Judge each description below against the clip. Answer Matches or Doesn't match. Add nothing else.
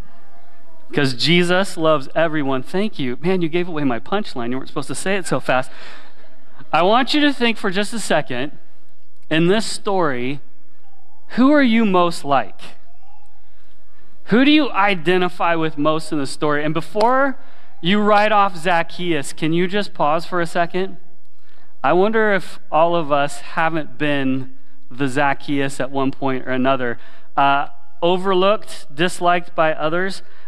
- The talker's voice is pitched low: Doesn't match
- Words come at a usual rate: Matches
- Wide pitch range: Matches